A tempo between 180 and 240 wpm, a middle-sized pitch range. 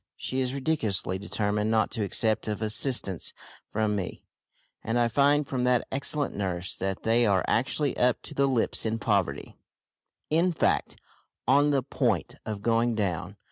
No: average, 160 wpm; average, 4.4 semitones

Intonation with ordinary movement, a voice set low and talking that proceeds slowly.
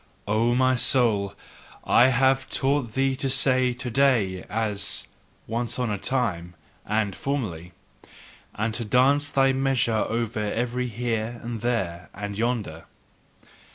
Yes: average, 3.6 semitones; low, 120 Hz; slow, 130 wpm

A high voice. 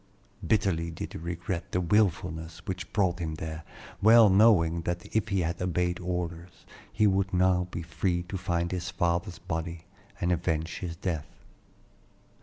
No: very low, 90 Hz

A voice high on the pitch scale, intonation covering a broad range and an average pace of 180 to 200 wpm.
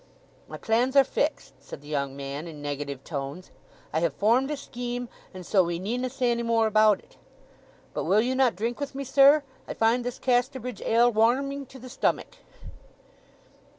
Yes: high, 235 Hz; wide, 6.4 semitones; average, 185 wpm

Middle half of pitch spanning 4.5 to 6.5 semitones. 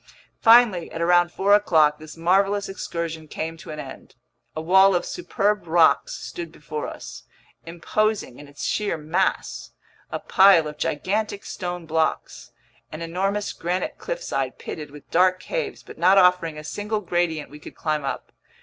No: average, 3.8 semitones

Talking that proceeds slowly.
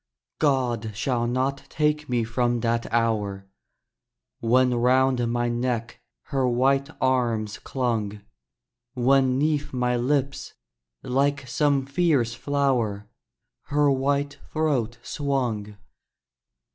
Yes: slow, 100 wpm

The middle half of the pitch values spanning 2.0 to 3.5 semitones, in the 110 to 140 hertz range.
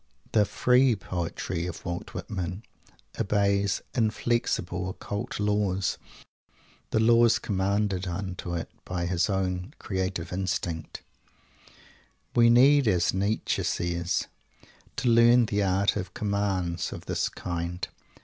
No: average, 3.1 semitones; very low, 95 Hz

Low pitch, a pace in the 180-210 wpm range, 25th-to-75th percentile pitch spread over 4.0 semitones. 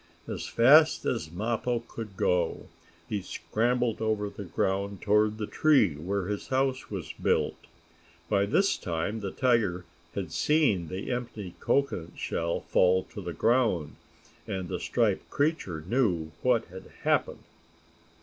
No: low, 105 Hz; average, 140 wpm; average, 5.0 semitones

